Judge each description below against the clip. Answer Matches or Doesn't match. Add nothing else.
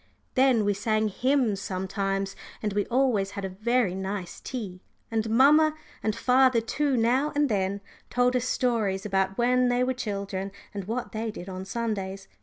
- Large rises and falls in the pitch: Doesn't match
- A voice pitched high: Matches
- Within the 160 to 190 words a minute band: Matches